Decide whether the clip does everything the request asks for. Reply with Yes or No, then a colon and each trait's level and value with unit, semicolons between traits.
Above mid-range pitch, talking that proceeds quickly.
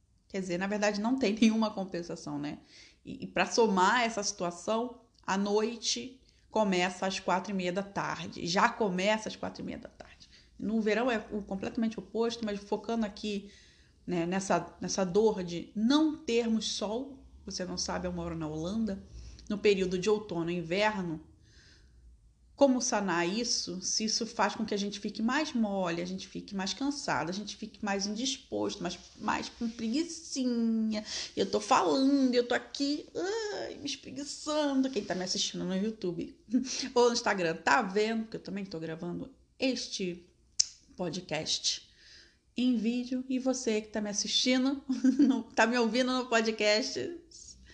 No: high, 215 Hz; average, 165 wpm